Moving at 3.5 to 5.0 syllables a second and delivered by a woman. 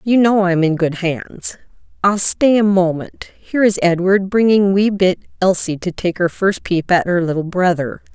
Yes: 4.7 syllables/s; female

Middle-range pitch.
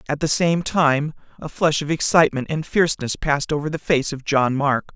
Yes: medium, 150 Hz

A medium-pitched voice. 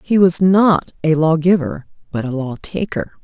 Yes: medium, 165 Hz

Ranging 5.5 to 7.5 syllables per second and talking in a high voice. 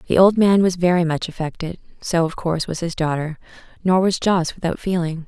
No: 5.6 syllables/s; medium, 175 Hz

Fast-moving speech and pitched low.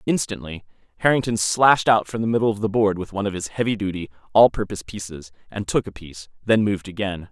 Yes: fast, 215 wpm; low, 100 Hz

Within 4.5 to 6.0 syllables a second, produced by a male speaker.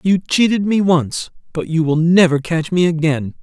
Yes: 4.6 syllables/s; male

